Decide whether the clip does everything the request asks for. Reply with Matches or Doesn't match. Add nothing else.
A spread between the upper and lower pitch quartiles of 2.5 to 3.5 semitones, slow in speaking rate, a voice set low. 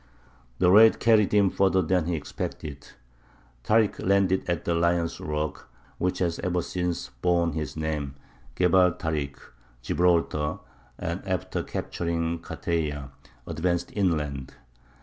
Matches